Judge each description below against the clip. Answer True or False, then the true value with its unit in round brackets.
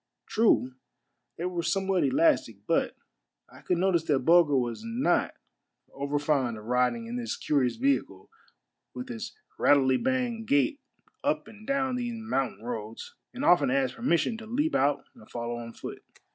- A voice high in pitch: False (175 Hz)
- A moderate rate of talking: True (160 wpm)